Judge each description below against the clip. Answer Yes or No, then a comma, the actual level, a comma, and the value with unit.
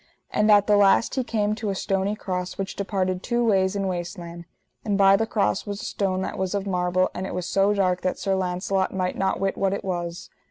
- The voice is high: Yes, high, 195 Hz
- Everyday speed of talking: No, fast, 240 wpm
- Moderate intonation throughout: No, narrow, 1.8 semitones